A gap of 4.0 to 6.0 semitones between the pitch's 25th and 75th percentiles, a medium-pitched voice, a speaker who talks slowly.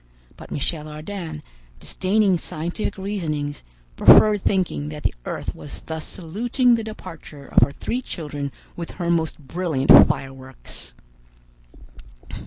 Yes: average, 4.8 semitones; medium, 160 Hz; slow, 120 wpm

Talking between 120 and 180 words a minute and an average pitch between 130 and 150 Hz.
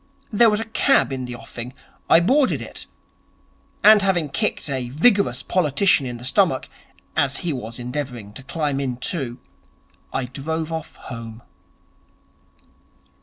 Yes: average, 140 wpm; medium, 140 Hz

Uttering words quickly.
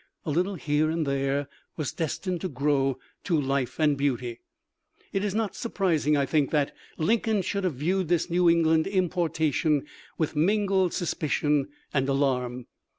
No: average, 150 wpm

